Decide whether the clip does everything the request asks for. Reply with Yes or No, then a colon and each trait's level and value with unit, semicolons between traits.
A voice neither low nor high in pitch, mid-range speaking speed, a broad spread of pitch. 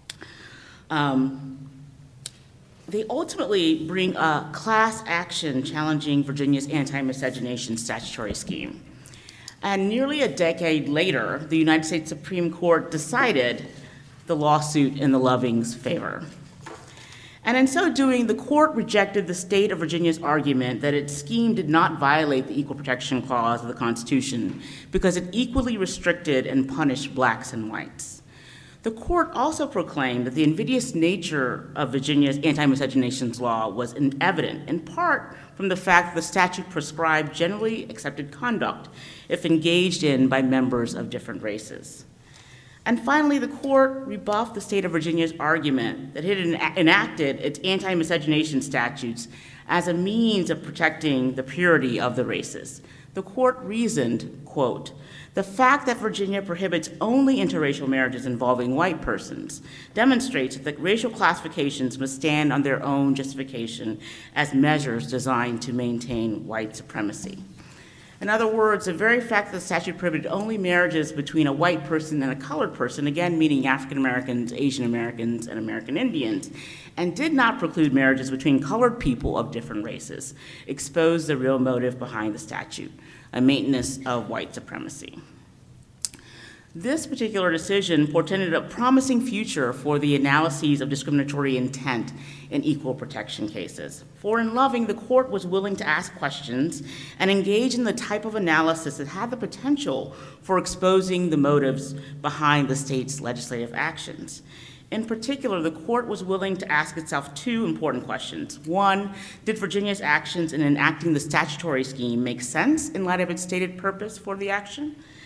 Yes: medium, 155 Hz; average, 155 wpm; wide, 6.3 semitones